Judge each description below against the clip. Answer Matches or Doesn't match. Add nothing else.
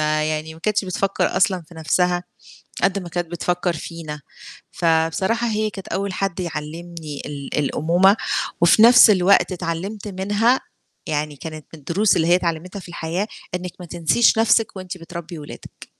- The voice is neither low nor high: Matches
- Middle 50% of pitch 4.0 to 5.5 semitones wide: Doesn't match